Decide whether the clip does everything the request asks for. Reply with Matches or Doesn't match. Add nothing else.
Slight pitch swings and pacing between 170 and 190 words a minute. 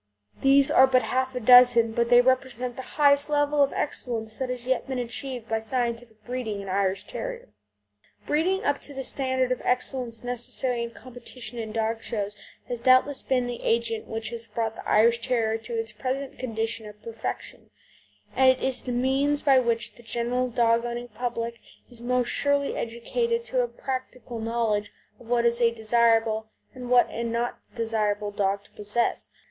Matches